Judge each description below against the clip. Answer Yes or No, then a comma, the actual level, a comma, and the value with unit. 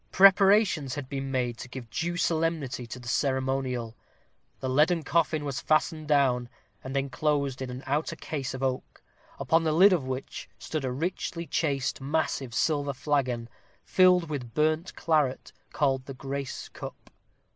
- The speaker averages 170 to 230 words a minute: No, average, 155 wpm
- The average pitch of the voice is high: No, medium, 140 Hz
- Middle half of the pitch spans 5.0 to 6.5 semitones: No, average, 3.3 semitones